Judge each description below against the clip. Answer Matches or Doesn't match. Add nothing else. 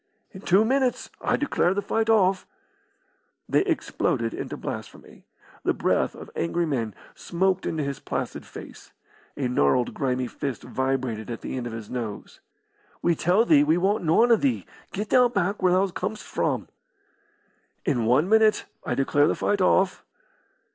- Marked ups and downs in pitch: Matches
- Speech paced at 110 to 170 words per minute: Matches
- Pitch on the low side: Doesn't match